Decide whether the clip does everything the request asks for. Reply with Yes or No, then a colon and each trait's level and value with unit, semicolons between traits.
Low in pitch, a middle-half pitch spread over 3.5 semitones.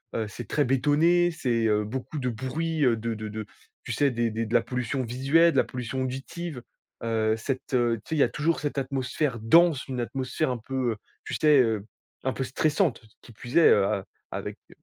Yes: low, 130 Hz; average, 4.1 semitones